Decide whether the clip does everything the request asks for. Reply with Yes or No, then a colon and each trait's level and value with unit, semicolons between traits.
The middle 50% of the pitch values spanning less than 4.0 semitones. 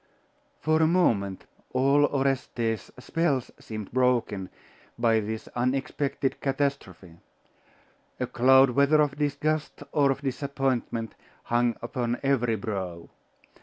Yes: average, 3.6 semitones